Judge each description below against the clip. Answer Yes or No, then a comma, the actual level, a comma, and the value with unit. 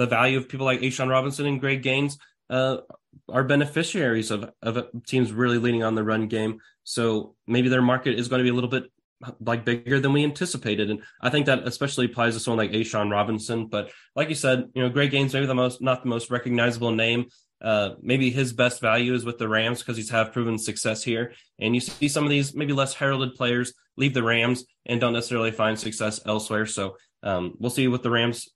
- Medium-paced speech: No, fast, 225 wpm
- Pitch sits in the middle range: No, low, 120 Hz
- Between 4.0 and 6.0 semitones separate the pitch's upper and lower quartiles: No, narrow, 2.5 semitones